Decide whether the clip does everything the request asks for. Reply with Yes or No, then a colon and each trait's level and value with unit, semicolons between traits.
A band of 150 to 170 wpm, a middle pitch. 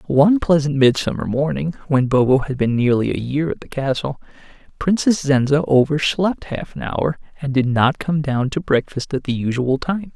No: average, 190 wpm; medium, 145 Hz